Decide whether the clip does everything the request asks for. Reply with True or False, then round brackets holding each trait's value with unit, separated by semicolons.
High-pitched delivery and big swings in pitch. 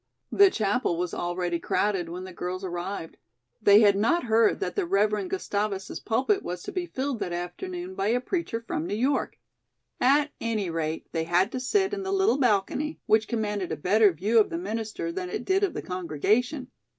True (210 Hz; 6.6 semitones)